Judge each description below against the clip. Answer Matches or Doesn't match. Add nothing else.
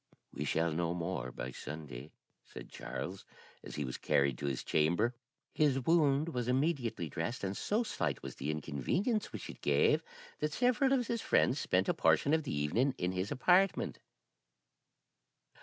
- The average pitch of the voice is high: Doesn't match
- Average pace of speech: Matches